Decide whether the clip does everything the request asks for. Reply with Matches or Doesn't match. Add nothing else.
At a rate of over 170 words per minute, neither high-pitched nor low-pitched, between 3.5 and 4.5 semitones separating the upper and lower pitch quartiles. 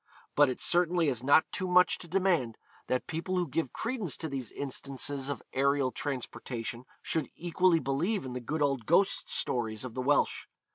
Doesn't match